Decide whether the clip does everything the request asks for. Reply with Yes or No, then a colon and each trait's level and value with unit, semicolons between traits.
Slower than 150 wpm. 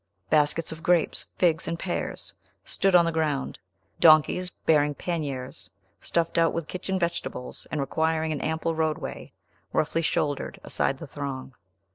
Yes: average, 140 wpm